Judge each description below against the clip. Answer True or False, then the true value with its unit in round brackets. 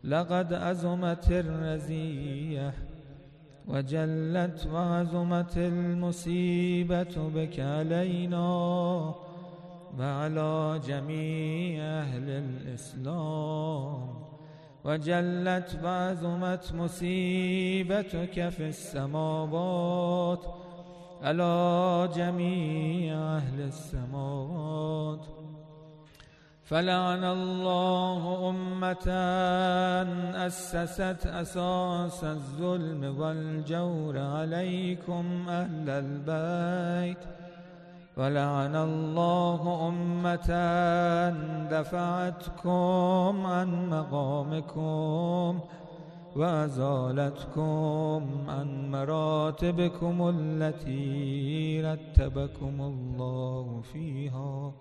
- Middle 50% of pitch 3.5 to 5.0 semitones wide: False (2.4 semitones)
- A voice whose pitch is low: False (170 Hz)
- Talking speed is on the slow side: True (50 wpm)